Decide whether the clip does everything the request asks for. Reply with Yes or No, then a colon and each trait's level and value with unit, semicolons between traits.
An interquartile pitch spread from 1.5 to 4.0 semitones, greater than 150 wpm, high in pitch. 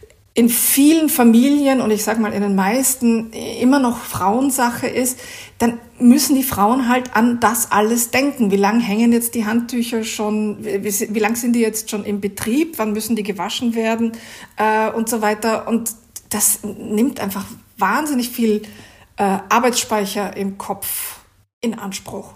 Yes: narrow, 2.5 semitones; average, 165 wpm; high, 225 Hz